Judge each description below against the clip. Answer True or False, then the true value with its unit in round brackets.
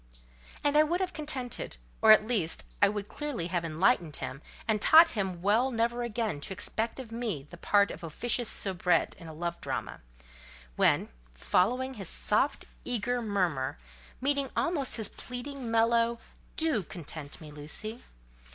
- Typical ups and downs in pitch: False (6.0 semitones)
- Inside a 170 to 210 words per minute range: False (150 wpm)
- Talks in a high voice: True (220 Hz)